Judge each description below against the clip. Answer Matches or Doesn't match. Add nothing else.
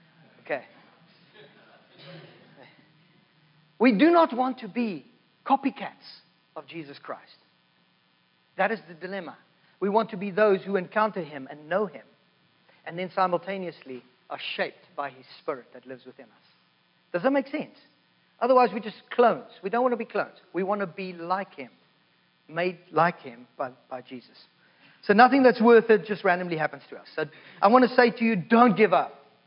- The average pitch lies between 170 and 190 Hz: Matches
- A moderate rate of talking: Matches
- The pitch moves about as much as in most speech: Doesn't match